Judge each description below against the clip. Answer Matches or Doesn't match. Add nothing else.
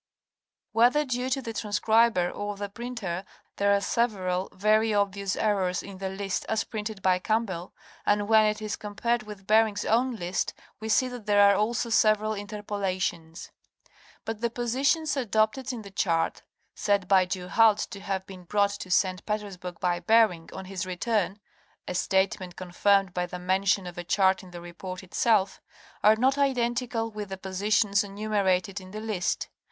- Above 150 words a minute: Matches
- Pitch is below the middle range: Doesn't match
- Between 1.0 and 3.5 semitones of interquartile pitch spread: Matches